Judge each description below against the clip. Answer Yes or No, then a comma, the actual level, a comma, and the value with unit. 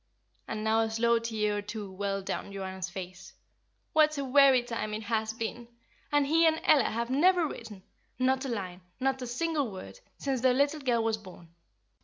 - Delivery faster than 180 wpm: Yes, average, 190 wpm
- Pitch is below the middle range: No, high, 230 Hz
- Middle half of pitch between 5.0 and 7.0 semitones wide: No, average, 4.5 semitones